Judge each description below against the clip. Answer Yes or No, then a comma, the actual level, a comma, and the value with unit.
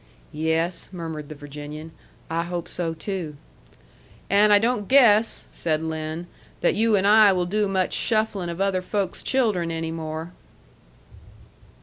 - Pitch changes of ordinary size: Yes, average, 4.2 semitones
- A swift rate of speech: No, average, 140 wpm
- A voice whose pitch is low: No, medium, 175 Hz